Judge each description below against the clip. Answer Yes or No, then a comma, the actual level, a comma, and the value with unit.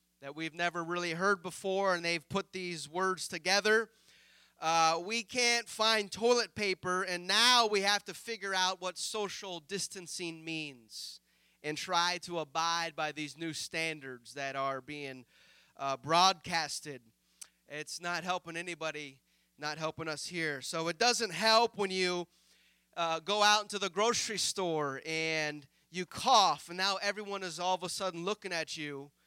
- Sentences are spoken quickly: No, average, 160 wpm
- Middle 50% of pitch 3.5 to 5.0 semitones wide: Yes, average, 4.0 semitones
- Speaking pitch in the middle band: Yes, medium, 175 Hz